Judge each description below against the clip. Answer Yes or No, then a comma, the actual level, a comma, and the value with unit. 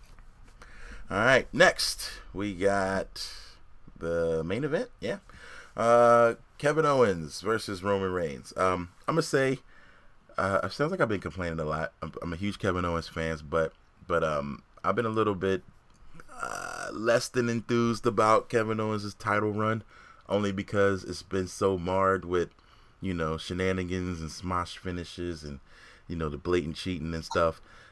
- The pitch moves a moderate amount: Yes, average, 3.9 semitones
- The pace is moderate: Yes, average, 155 wpm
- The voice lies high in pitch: No, very low, 95 Hz